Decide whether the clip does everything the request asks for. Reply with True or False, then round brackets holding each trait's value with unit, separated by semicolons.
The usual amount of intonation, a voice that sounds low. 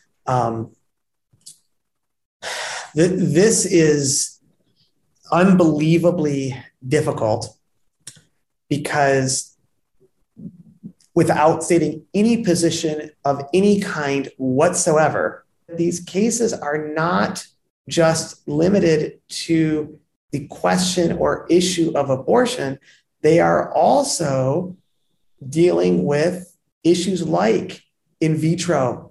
False (3.5 semitones; 160 Hz)